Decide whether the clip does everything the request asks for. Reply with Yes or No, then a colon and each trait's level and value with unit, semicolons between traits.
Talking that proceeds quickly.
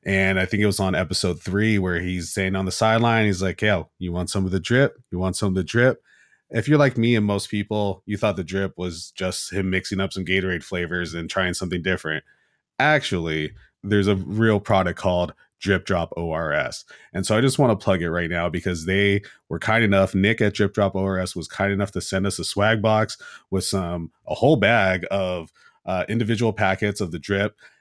Yes: fast, 220 wpm